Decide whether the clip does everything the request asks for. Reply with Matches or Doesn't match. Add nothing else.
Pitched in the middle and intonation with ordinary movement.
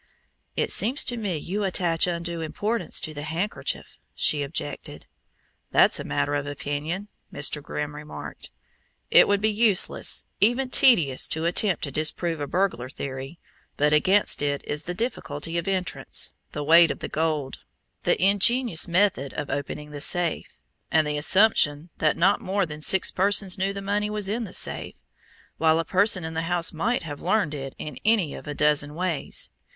Matches